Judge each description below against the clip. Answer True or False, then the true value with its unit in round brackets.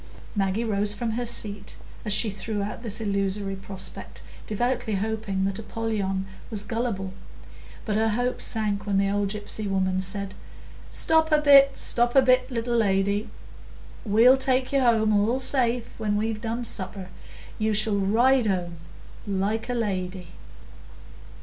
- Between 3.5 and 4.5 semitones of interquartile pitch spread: False (3.1 semitones)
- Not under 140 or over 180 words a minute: True (150 wpm)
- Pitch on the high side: True (215 Hz)